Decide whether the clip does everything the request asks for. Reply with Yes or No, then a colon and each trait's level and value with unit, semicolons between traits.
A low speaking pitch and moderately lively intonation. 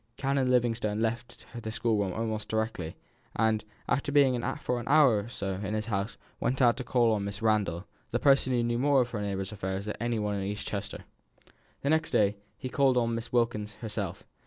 Yes: low, 115 Hz; average, 3.0 semitones